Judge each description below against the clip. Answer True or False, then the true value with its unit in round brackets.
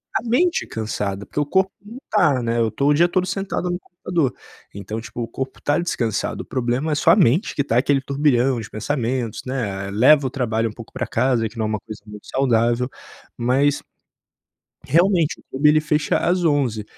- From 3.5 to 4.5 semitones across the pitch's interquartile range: False (5.0 semitones)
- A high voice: False (130 Hz)